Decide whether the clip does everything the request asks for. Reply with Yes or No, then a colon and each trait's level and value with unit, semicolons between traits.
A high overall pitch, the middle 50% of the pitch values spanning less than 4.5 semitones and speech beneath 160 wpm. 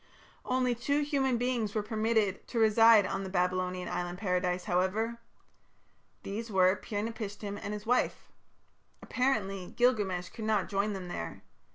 Yes: high, 210 Hz; average, 3.7 semitones; average, 145 wpm